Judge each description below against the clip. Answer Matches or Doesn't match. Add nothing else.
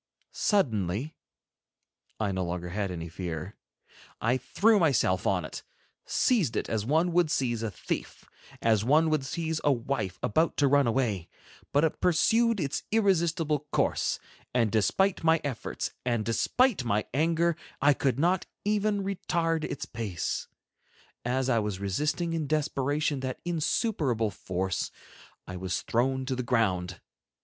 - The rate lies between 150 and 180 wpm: Doesn't match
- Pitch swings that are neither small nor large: Doesn't match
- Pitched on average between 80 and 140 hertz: Matches